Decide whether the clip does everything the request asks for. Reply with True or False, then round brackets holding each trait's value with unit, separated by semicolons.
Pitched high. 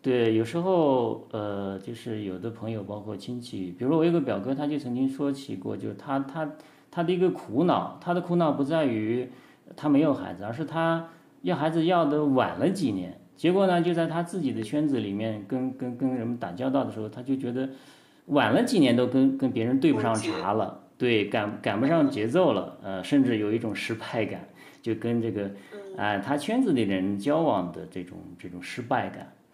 False (130 Hz)